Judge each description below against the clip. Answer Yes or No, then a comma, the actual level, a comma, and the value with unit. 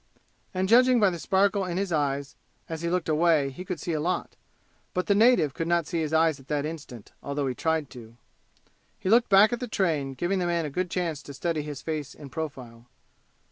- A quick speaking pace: Yes, fast, 220 wpm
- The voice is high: No, medium, 165 Hz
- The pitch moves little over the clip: No, average, 4.1 semitones